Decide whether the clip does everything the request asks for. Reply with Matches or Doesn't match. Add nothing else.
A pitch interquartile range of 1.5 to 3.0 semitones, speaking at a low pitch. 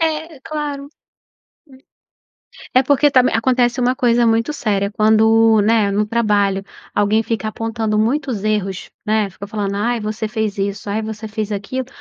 Doesn't match